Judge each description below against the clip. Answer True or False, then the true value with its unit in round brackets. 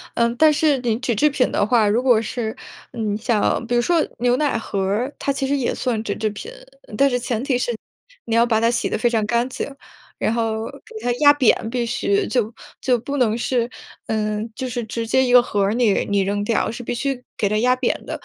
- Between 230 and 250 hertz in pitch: True (240 Hz)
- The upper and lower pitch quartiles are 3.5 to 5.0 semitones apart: False (2.7 semitones)